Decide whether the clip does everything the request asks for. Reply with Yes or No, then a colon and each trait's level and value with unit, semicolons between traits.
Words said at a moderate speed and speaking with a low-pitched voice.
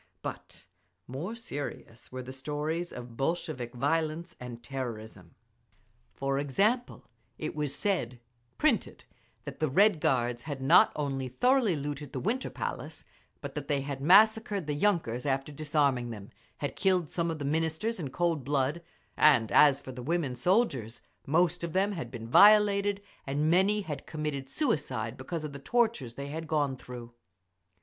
No: average, 155 wpm; medium, 150 Hz